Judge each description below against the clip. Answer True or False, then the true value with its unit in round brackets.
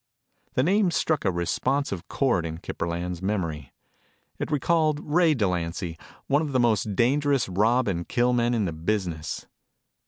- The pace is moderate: True (155 wpm)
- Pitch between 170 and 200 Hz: False (110 Hz)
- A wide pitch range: True (8.2 semitones)